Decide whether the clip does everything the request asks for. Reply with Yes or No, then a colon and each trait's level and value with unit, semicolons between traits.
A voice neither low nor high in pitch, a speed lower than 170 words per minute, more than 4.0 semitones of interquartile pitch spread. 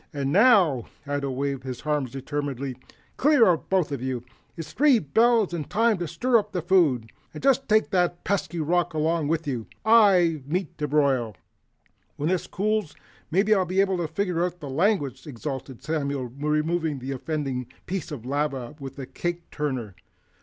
No: medium, 155 Hz; average, 175 wpm; average, 5.3 semitones